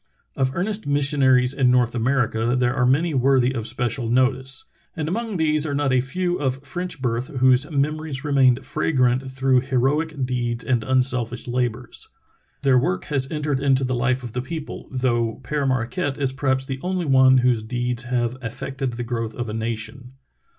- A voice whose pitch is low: Yes, low, 130 Hz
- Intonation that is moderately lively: No, narrow, 2.3 semitones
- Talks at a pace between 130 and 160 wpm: No, average, 180 wpm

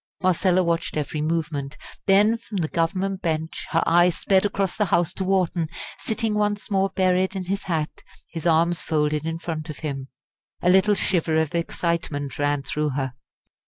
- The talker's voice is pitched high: No, medium, 170 Hz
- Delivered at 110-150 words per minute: No, average, 170 wpm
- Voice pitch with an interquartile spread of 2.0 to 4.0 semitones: Yes, average, 3.4 semitones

